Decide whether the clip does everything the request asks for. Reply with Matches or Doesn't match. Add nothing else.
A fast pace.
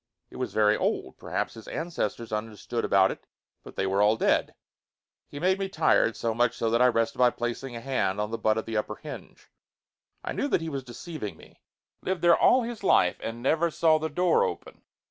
Matches